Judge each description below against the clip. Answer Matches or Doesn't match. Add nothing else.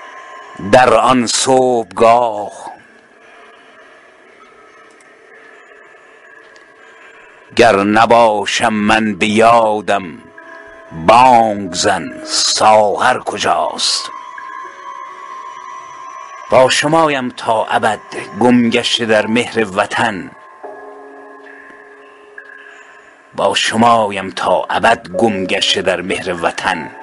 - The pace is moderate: Doesn't match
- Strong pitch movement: Matches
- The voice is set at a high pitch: Doesn't match